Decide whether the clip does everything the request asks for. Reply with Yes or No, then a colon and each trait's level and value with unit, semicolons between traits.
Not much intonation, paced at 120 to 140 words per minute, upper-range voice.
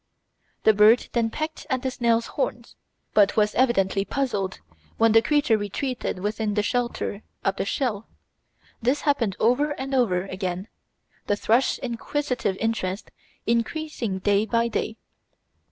No: average, 3.8 semitones; slow, 135 wpm; high, 225 Hz